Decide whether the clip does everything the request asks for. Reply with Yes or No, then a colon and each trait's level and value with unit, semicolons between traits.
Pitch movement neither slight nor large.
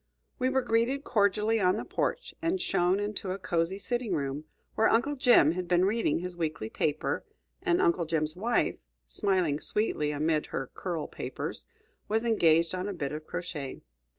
No: wide, 6.1 semitones